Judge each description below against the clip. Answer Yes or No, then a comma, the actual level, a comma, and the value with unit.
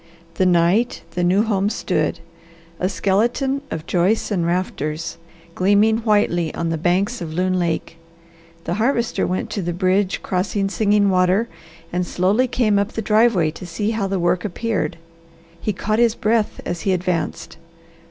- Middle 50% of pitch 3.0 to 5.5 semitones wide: Yes, average, 3.5 semitones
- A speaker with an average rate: Yes, average, 160 wpm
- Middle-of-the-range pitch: No, high, 195 Hz